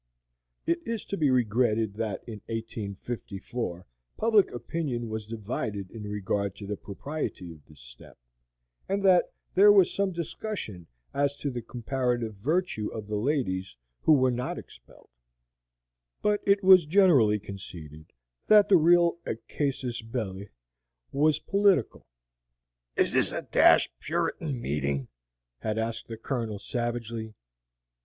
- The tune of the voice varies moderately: No, wide, 7.2 semitones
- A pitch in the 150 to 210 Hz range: No, low, 120 Hz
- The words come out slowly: Yes, slow, 130 wpm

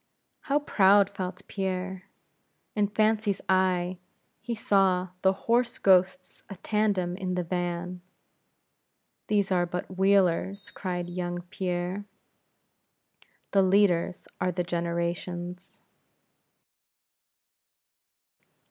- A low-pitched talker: No, medium, 185 Hz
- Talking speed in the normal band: No, slow, 95 wpm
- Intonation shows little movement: Yes, narrow, 2.0 semitones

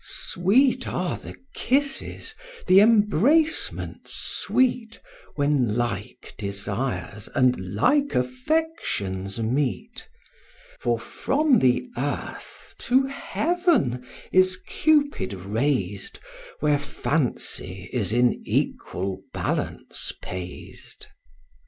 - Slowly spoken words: Yes, slow, 85 wpm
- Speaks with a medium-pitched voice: Yes, medium, 145 Hz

